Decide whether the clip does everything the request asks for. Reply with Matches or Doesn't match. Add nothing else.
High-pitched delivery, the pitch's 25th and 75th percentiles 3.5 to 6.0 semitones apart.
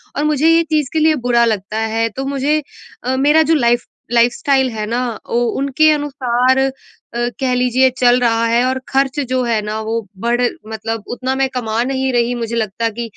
Doesn't match